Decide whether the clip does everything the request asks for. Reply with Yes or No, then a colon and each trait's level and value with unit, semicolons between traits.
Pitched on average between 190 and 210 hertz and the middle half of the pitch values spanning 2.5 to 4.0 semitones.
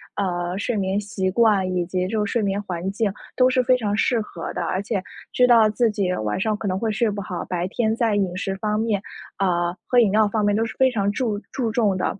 Yes: high, 205 Hz; average, 2.9 semitones